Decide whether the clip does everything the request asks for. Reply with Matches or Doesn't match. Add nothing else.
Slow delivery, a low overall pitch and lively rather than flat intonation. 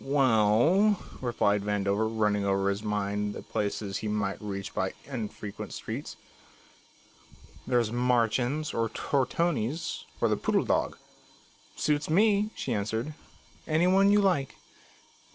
Matches